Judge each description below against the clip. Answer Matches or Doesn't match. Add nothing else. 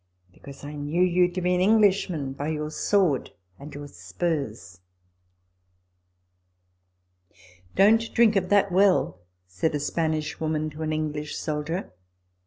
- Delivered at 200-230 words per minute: Doesn't match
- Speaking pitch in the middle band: Matches